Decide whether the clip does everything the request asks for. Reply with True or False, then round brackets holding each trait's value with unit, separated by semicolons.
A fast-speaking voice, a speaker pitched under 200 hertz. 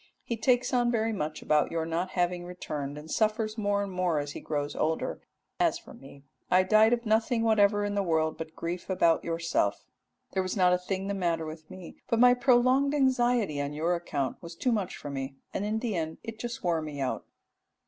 True (215 wpm; 185 Hz)